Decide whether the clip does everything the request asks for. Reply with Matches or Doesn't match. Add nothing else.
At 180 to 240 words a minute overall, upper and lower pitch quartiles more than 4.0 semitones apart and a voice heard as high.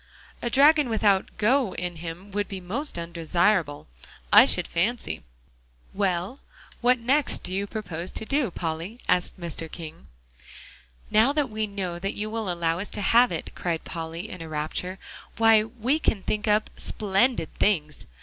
Doesn't match